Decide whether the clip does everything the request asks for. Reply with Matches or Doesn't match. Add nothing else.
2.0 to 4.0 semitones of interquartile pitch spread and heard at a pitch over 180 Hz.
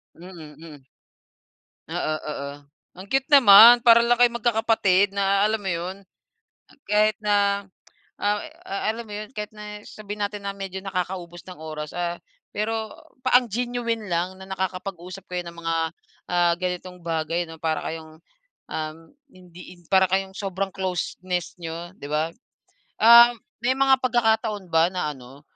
Matches